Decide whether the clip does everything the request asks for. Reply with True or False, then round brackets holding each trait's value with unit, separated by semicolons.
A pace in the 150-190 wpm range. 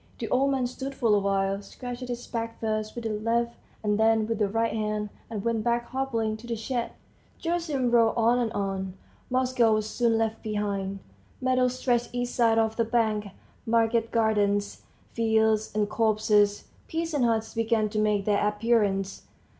True (170 wpm)